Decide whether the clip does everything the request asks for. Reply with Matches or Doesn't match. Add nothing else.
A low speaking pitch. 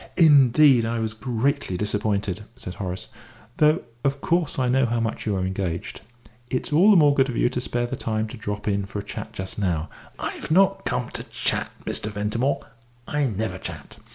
Matches